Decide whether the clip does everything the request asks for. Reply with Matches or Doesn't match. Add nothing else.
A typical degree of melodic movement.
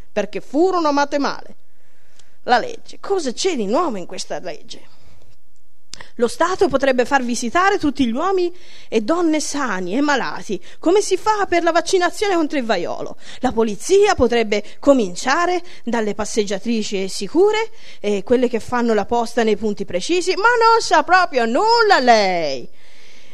Doesn't match